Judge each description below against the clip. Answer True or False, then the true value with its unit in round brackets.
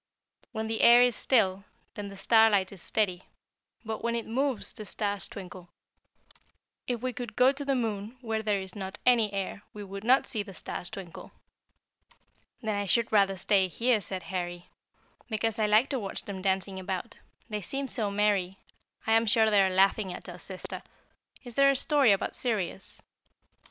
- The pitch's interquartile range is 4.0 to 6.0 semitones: False (3.2 semitones)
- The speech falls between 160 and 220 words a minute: True (180 wpm)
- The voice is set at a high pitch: True (210 Hz)